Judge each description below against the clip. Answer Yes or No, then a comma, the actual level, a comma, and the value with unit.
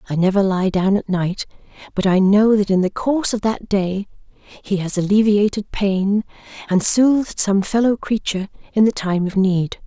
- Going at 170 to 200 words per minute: Yes, average, 180 wpm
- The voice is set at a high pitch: Yes, high, 200 Hz